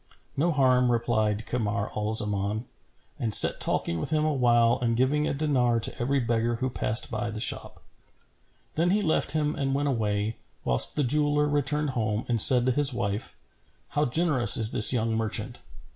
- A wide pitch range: No, average, 4.6 semitones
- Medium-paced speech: Yes, average, 175 wpm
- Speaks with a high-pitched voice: No, low, 120 Hz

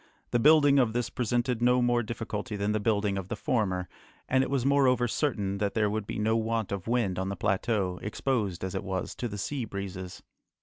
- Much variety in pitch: No, average, 3.7 semitones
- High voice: No, low, 110 Hz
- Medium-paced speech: No, fast, 215 wpm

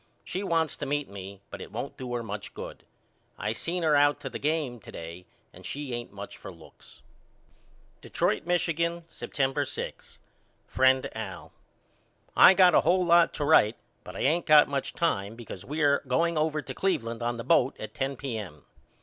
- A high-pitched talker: No, low, 135 Hz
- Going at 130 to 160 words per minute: No, average, 185 wpm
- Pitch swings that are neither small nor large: No, wide, 5.7 semitones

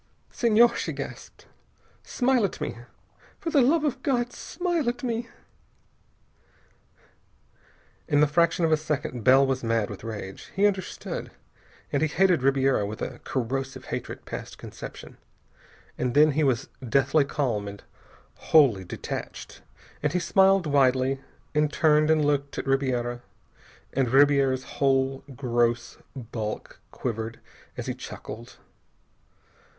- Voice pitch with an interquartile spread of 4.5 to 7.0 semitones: Yes, average, 5.2 semitones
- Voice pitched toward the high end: No, medium, 140 Hz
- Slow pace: Yes, slow, 130 wpm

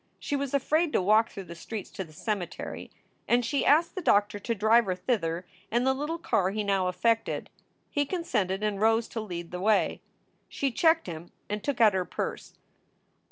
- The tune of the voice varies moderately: No, wide, 5.8 semitones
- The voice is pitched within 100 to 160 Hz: No, high, 215 Hz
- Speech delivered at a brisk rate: No, average, 195 wpm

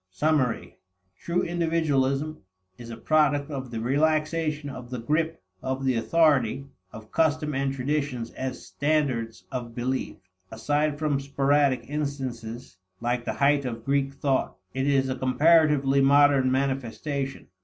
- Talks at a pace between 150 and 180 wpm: No, slow, 135 wpm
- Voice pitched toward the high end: No, medium, 140 Hz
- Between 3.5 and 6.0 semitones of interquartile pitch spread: No, average, 2.7 semitones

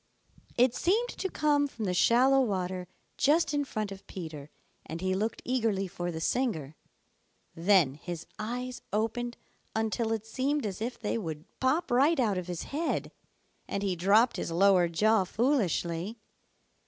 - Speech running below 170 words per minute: Yes, average, 155 wpm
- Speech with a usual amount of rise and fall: No, wide, 5.8 semitones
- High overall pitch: Yes, high, 215 Hz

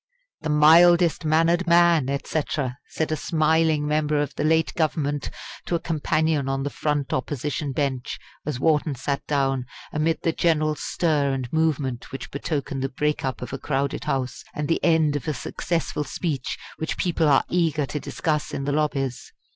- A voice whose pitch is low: No, medium, 150 Hz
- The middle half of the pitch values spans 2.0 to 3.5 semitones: Yes, narrow, 2.6 semitones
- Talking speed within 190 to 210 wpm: No, average, 175 wpm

